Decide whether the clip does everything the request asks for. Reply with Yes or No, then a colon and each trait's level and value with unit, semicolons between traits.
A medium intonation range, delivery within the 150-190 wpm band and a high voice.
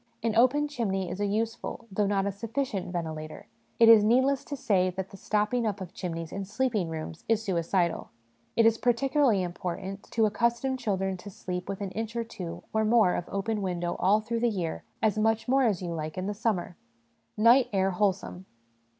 No: average, 3.8 semitones; average, 200 wpm; high, 205 Hz